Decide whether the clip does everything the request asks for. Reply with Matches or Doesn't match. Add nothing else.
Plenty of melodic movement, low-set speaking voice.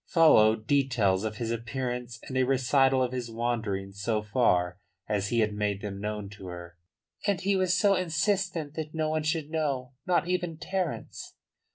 Matches